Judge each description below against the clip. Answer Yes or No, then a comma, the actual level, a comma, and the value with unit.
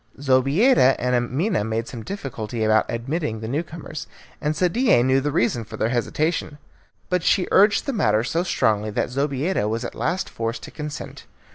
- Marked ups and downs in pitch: Yes, wide, 6.4 semitones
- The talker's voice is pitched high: No, low, 135 Hz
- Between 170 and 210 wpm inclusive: Yes, average, 175 wpm